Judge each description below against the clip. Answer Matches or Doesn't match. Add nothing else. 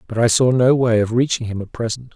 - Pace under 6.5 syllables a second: Matches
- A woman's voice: Doesn't match